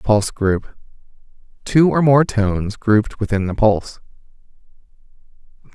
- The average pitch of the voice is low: Yes, low, 110 Hz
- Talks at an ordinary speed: No, slow, 105 wpm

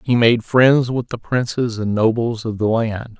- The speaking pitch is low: Yes, low, 115 Hz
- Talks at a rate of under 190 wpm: No, fast, 205 wpm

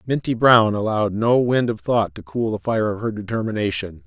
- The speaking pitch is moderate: No, low, 115 Hz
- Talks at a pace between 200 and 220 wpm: Yes, fast, 205 wpm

